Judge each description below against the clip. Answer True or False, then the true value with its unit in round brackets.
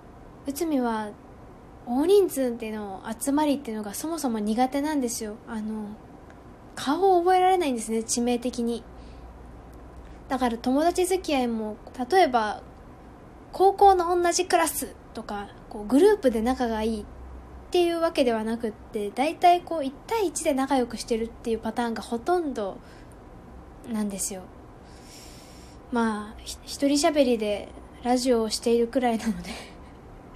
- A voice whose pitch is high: True (240 Hz)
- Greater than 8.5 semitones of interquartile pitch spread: False (5.3 semitones)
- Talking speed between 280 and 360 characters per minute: True (295 characters per minute)